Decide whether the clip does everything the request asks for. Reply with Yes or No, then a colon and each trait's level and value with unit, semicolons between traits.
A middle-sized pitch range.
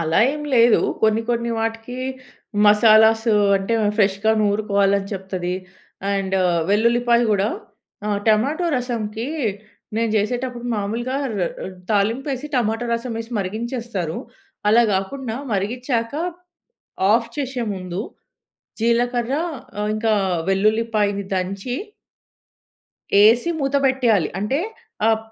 Yes: average, 3.0 semitones